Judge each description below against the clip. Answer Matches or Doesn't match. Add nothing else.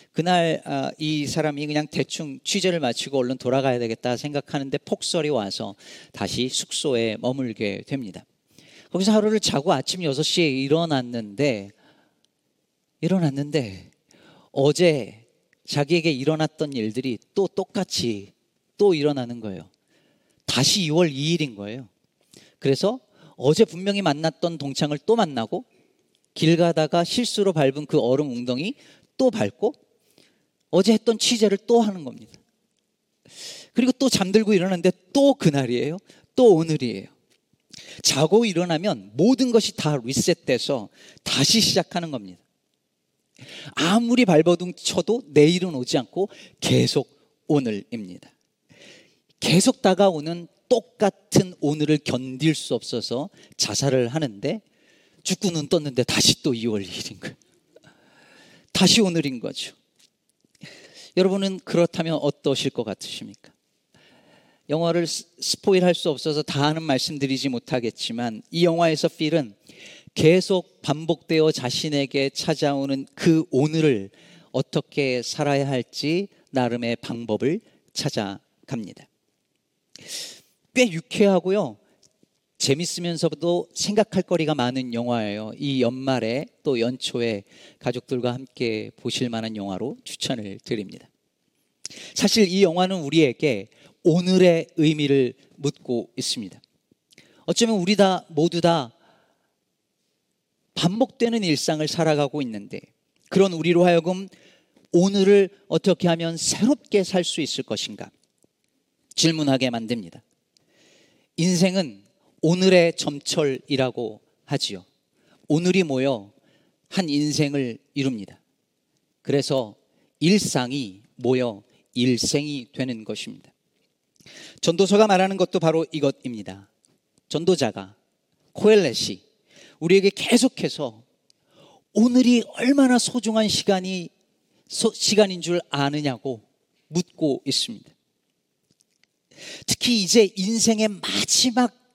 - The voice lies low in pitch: Doesn't match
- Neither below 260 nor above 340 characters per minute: Doesn't match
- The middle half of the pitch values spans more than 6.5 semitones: Doesn't match